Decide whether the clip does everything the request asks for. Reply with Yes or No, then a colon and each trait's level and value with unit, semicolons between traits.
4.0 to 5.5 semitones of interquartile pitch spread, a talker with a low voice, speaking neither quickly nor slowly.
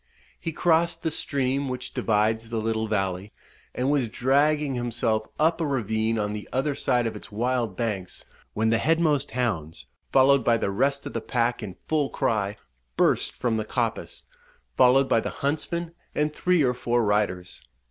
Yes: average, 4.3 semitones; low, 120 Hz; average, 170 wpm